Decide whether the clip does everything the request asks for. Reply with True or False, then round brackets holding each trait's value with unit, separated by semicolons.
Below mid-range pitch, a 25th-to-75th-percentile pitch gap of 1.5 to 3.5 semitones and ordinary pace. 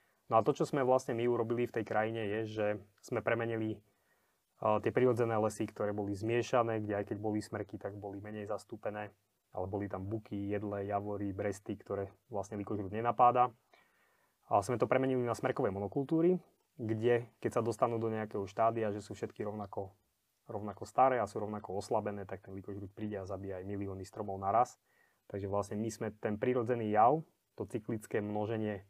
False (105 Hz; 2.4 semitones; 180 wpm)